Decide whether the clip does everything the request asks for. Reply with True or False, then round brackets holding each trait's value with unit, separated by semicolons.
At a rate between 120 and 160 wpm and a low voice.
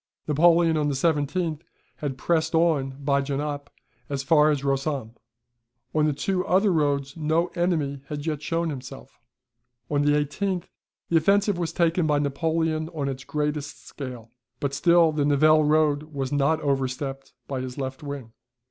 False (155 wpm; 150 Hz)